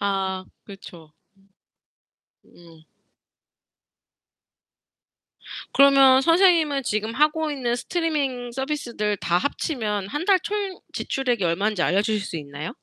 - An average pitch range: No, wide, 7.1 semitones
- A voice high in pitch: Yes, high, 240 Hz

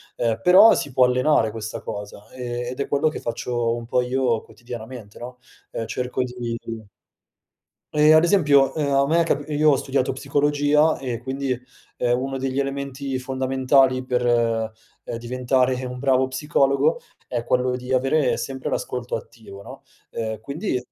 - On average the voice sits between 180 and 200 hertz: No, low, 130 Hz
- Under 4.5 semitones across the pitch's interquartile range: Yes, narrow, 2.4 semitones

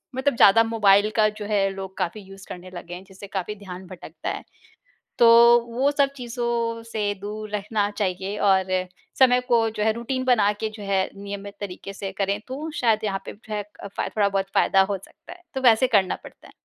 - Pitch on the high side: Yes, high, 205 Hz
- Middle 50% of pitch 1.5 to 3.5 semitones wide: Yes, average, 2.8 semitones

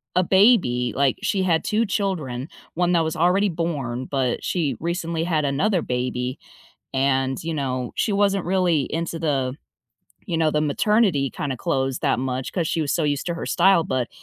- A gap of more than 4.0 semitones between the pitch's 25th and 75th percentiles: Yes, average, 5.1 semitones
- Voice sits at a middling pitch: Yes, medium, 160 Hz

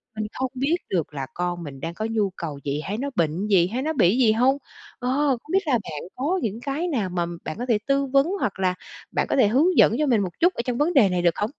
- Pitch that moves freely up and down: Yes, wide, 7.5 semitones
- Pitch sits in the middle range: No, high, 220 Hz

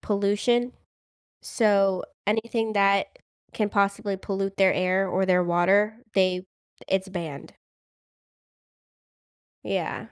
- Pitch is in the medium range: No, high, 195 Hz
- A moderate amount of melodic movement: No, narrow, 1.8 semitones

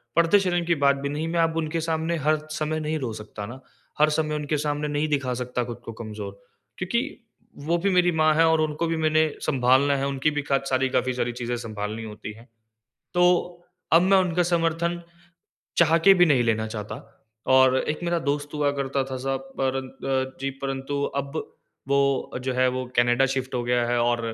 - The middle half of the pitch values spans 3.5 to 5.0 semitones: Yes, average, 3.8 semitones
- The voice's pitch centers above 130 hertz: Yes, medium, 140 Hz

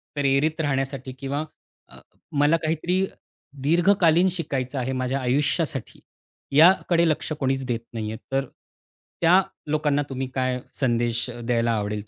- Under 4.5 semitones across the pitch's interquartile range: Yes, average, 3.6 semitones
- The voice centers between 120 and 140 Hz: Yes, low, 135 Hz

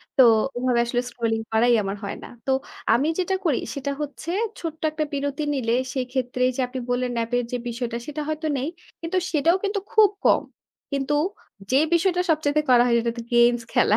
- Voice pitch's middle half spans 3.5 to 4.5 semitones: Yes, average, 4.2 semitones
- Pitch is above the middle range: Yes, very high, 260 Hz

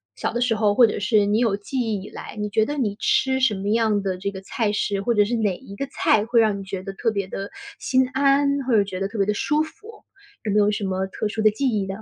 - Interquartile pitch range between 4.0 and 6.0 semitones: No, average, 3.2 semitones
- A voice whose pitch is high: Yes, high, 210 Hz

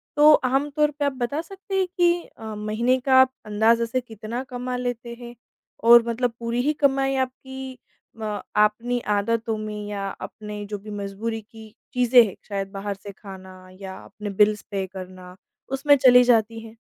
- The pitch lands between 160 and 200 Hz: No, high, 230 Hz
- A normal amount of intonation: Yes, average, 3.6 semitones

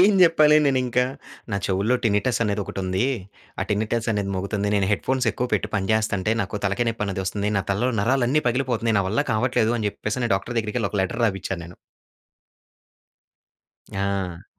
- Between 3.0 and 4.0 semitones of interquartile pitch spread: Yes, average, 3.6 semitones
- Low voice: Yes, low, 105 Hz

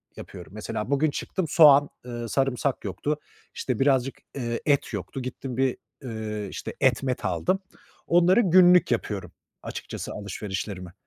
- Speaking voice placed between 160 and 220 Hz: No, low, 130 Hz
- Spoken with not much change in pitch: No, average, 5.1 semitones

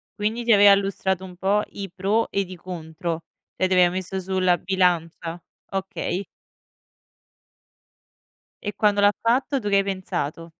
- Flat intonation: Yes, narrow, 2.3 semitones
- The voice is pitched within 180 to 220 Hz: Yes, high, 190 Hz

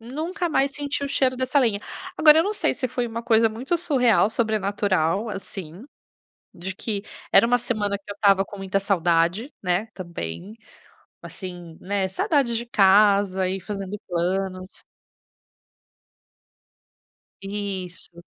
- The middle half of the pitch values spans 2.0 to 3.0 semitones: No, average, 4.2 semitones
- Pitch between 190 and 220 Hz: Yes, high, 205 Hz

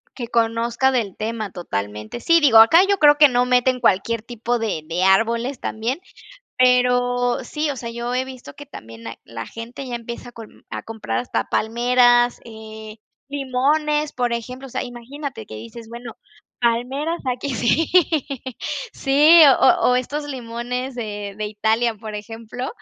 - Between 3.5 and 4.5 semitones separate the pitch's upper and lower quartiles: No, average, 2.7 semitones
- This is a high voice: Yes, high, 240 Hz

